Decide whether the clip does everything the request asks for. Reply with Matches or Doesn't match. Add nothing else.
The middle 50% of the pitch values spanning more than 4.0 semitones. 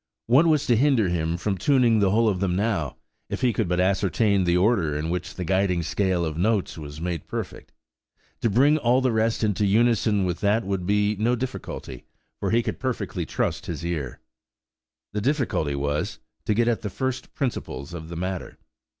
Matches